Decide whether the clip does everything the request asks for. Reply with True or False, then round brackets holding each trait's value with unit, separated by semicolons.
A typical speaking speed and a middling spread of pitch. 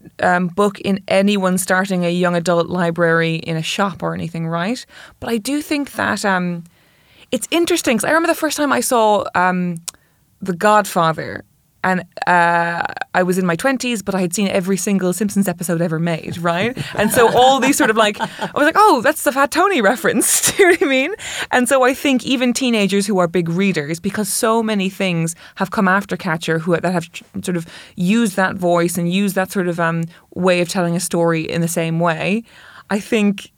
False (210 wpm; 4.9 semitones)